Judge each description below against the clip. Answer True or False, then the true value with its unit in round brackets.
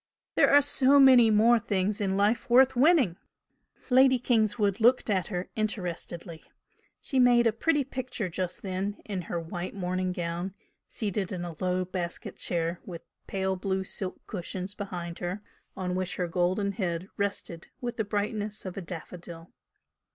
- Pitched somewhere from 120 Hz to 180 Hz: False (195 Hz)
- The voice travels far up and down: False (3.8 semitones)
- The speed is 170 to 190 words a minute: False (160 wpm)